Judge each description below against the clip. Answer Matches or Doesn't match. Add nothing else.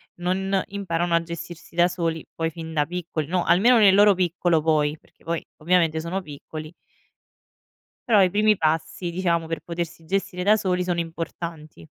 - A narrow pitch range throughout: Matches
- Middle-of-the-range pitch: Matches